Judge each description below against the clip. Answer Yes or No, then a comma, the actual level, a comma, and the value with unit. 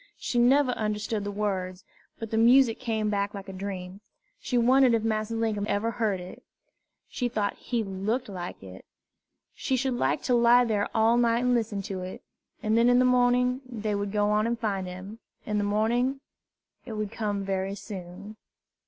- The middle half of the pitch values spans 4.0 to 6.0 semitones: No, average, 3.1 semitones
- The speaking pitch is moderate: No, high, 215 Hz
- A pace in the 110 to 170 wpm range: No, average, 190 wpm